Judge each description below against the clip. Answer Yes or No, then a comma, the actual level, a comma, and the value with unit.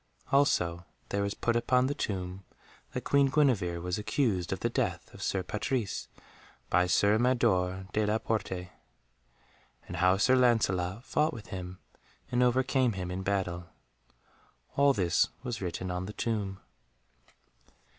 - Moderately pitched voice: No, low, 100 Hz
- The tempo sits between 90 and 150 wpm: Yes, average, 145 wpm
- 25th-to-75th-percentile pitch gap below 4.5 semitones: No, average, 5.1 semitones